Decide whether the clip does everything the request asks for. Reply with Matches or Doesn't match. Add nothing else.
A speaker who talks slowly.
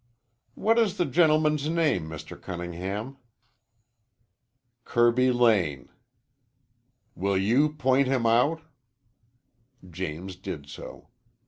Matches